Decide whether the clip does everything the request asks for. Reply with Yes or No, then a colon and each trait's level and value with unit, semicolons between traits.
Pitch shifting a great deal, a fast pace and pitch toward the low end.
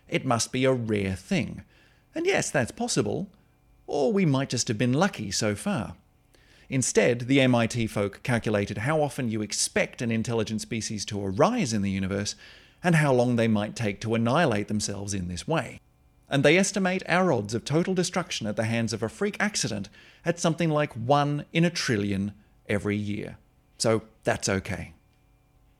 No: wide, 6.1 semitones; average, 175 wpm; low, 115 Hz